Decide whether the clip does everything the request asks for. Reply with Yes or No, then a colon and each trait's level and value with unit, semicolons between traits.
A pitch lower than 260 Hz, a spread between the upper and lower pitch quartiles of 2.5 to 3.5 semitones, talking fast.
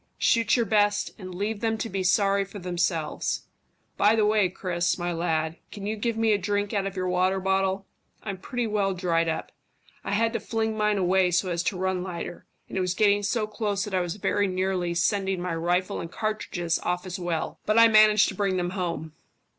Yes: high, 190 Hz; average, 2.8 semitones; fast, 215 wpm